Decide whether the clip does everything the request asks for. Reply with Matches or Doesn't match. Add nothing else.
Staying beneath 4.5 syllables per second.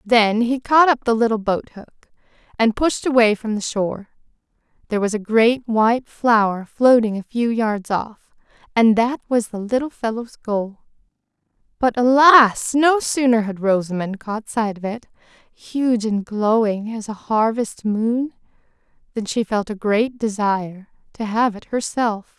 Matches